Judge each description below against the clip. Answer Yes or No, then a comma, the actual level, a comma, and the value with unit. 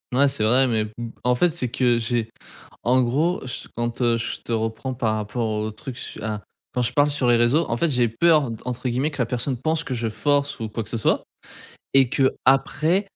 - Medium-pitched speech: No, low, 125 Hz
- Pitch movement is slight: No, average, 3.5 semitones